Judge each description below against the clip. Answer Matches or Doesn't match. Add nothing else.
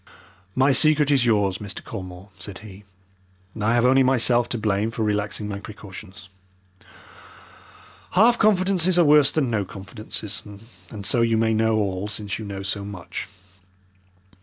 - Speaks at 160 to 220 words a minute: Doesn't match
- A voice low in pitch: Matches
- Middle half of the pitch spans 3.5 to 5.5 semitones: Matches